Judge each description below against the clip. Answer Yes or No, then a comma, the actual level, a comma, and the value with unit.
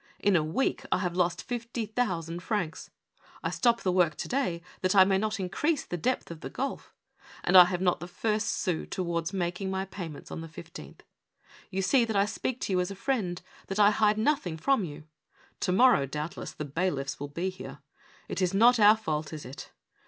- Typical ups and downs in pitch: Yes, average, 4.2 semitones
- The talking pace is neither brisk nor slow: No, fast, 210 wpm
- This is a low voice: No, medium, 185 Hz